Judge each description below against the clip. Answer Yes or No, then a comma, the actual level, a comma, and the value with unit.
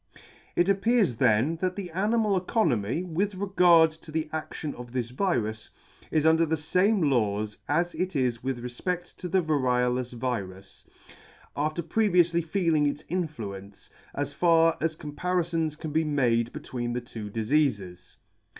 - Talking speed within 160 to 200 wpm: No, average, 145 wpm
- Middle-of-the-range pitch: Yes, medium, 155 Hz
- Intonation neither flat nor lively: No, wide, 6.3 semitones